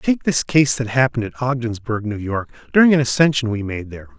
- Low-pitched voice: Yes, low, 120 Hz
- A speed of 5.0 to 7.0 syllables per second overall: Yes, 5.9 syllables/s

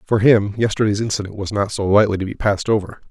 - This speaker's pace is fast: Yes, fast, 230 wpm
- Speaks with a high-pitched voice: No, low, 105 Hz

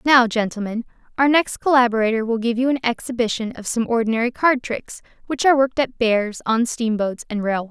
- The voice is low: No, high, 235 Hz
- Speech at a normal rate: Yes, average, 185 wpm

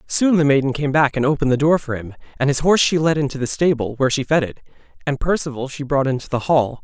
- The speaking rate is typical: No, fast, 265 wpm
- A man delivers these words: Yes, male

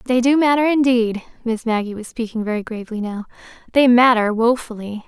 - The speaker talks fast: No, average, 155 wpm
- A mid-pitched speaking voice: No, high, 235 Hz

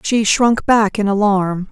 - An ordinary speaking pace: Yes, average, 175 wpm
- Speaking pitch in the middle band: No, high, 205 Hz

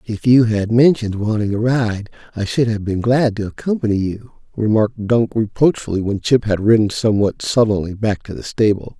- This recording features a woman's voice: No, male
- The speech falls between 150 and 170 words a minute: No, average, 185 wpm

